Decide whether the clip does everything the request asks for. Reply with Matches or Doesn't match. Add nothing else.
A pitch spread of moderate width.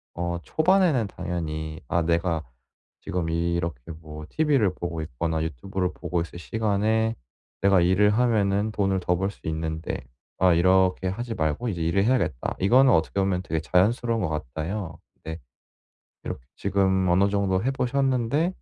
Matches